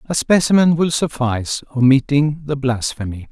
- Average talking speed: No, slow, 125 wpm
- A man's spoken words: Yes, male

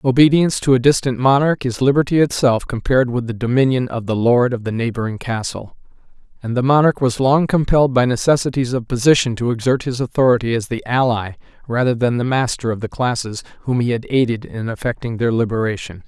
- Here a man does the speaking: Yes, male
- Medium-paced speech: Yes, average, 190 wpm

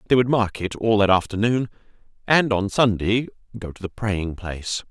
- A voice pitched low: Yes, low, 105 Hz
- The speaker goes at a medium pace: Yes, average, 170 wpm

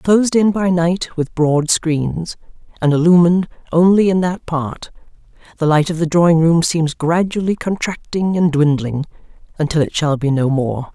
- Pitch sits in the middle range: Yes, medium, 165 Hz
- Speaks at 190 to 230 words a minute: No, average, 165 wpm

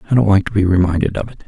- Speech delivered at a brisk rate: Yes, fast, 325 wpm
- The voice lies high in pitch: No, low, 100 Hz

